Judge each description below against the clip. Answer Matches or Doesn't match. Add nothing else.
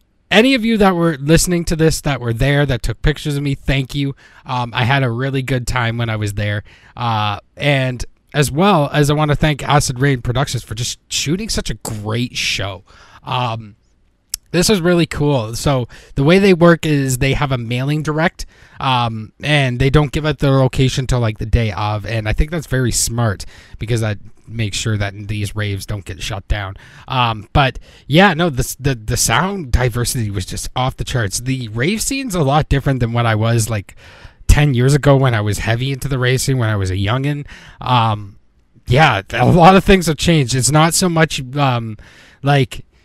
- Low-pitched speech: Matches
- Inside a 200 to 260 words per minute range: Matches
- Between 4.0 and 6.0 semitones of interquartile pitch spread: Matches